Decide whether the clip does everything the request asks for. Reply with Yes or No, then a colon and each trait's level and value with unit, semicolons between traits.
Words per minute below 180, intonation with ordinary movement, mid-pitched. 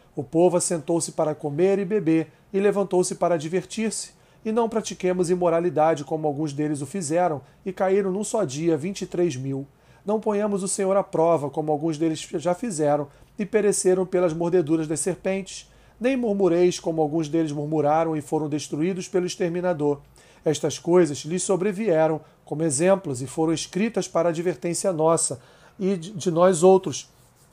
Yes: average, 160 wpm; average, 3.4 semitones; medium, 170 Hz